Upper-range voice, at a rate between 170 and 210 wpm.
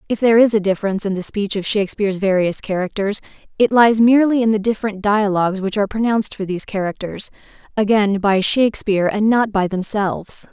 Yes: high, 205 Hz; average, 175 wpm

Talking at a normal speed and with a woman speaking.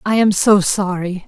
Yes: average, 190 wpm; female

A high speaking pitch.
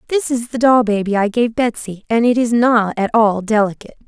Yes: high, 225 Hz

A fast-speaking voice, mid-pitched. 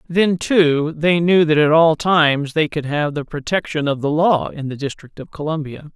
Yes: fast, 210 wpm; medium, 155 Hz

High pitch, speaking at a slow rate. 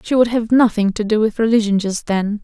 No: high, 215 Hz; fast, 245 wpm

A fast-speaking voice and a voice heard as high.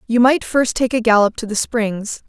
Yes: fast, 235 wpm; high, 230 Hz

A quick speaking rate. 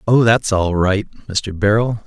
No: average, 175 wpm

